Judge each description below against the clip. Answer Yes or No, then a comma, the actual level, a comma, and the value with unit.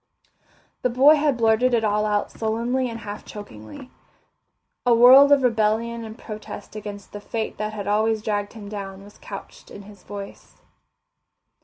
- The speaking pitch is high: Yes, high, 220 Hz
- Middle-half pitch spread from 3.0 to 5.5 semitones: No, narrow, 2.4 semitones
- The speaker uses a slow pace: No, average, 160 wpm